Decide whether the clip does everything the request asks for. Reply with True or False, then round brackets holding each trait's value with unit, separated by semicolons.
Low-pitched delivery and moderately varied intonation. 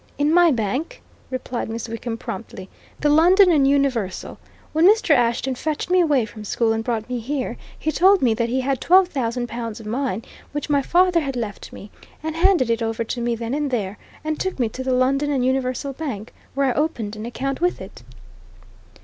False (260 Hz; 4.7 semitones)